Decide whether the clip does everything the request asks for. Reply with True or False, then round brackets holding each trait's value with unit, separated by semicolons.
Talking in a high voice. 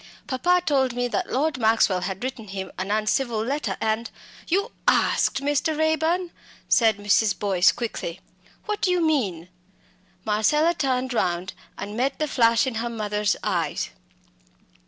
True (240 Hz)